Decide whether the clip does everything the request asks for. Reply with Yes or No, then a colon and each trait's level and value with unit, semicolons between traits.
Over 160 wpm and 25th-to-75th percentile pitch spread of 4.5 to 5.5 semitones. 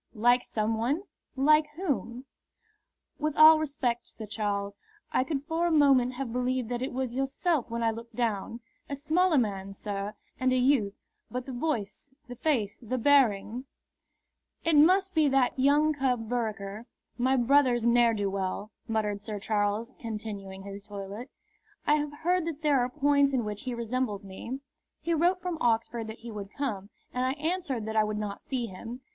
Yes: average, 180 wpm; average, 4.8 semitones